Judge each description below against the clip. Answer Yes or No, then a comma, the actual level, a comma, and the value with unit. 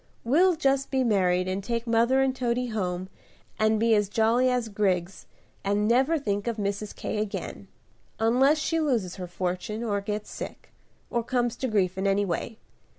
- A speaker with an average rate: Yes, average, 175 wpm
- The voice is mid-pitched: No, high, 220 Hz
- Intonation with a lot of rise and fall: No, average, 3.9 semitones